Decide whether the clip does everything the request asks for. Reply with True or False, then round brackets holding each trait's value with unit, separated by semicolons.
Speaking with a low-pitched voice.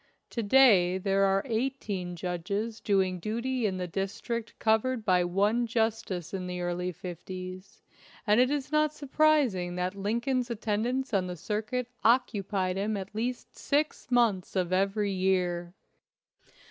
False (205 Hz)